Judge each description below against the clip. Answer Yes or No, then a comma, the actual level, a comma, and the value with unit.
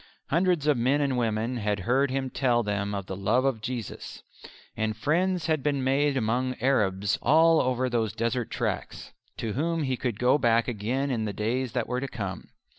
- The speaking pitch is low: Yes, low, 125 Hz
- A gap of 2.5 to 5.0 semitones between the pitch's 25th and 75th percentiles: Yes, average, 3.9 semitones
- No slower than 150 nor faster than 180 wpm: No, average, 190 wpm